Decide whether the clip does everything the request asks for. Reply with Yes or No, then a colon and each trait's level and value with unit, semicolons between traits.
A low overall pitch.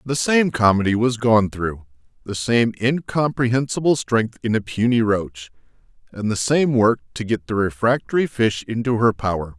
Yes: low, 115 Hz